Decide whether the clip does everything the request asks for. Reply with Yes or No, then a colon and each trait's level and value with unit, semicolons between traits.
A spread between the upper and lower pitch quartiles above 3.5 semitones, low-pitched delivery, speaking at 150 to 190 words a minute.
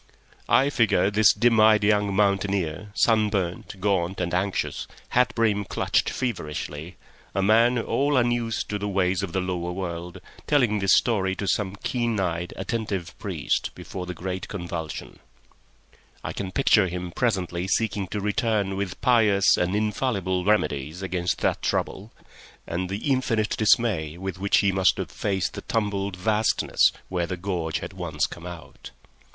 No: average, 3.1 semitones; low, 100 Hz; average, 155 wpm